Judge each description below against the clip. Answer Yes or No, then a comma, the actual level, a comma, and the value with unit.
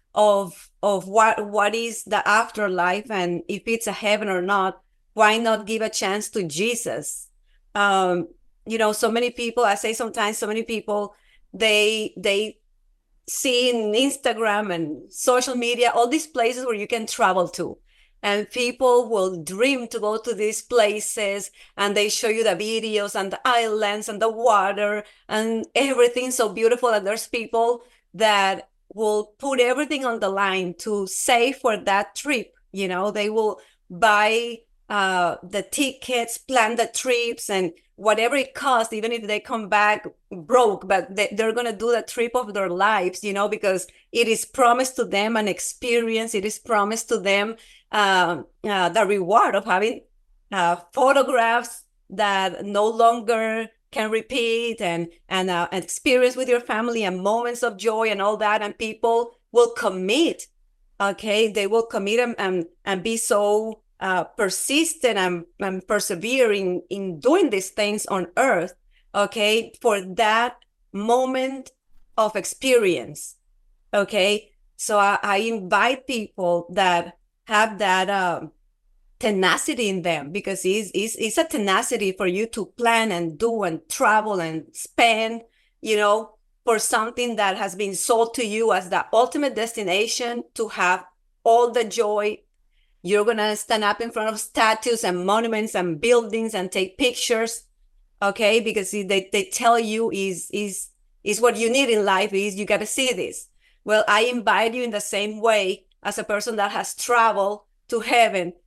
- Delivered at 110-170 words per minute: Yes, average, 160 wpm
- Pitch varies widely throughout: No, average, 2.8 semitones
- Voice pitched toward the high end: Yes, high, 215 Hz